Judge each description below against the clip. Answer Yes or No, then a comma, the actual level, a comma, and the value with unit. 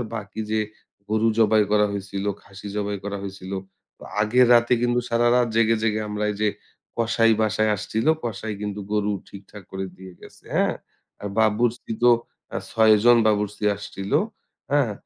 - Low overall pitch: Yes, low, 110 Hz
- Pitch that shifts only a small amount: Yes, narrow, 1.9 semitones